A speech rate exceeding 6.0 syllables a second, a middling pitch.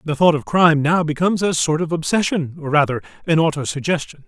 Yes: 6.3 syllables/s; medium, 160 Hz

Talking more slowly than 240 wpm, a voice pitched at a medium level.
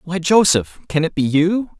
Yes: average, 200 wpm; medium, 170 Hz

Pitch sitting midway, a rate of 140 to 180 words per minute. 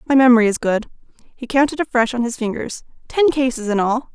No: high, 245 Hz; average, 175 wpm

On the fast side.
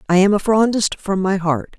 Yes: fast, 235 wpm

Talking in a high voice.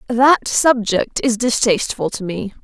Yes: high, 225 Hz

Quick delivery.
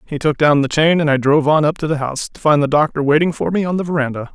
Yes: fast, 320 wpm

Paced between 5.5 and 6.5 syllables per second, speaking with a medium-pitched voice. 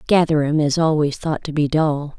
No: 4.9 syllables/s; medium, 150 Hz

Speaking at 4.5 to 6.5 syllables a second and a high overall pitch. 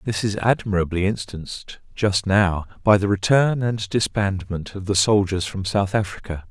No: 4.6 syllables/s; low, 100 Hz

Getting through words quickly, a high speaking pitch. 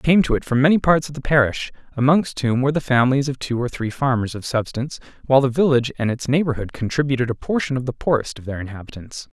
No: fast, 235 wpm; low, 130 Hz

